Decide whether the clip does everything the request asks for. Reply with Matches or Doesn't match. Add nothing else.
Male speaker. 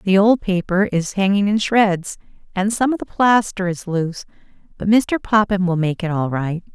Doesn't match